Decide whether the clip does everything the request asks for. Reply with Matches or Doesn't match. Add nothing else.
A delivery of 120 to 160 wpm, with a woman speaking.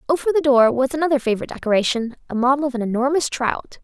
Doesn't match